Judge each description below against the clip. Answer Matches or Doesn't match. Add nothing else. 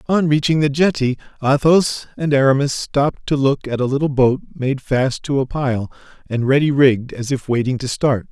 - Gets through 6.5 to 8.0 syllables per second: Doesn't match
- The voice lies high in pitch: Doesn't match